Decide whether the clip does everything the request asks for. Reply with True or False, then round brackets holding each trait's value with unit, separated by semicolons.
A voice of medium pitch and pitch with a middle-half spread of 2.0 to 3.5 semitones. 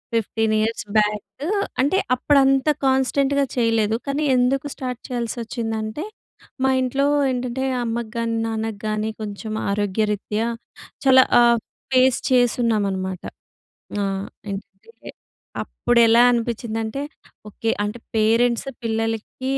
False (230 Hz; 2.8 semitones)